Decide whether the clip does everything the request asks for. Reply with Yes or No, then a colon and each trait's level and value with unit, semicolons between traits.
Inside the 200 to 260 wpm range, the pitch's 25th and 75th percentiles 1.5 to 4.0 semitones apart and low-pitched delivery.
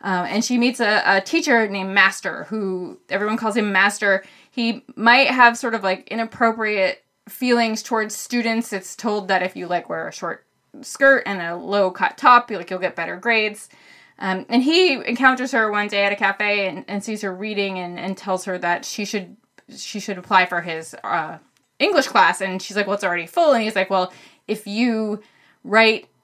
No: fast, 205 wpm; average, 3.3 semitones; high, 210 Hz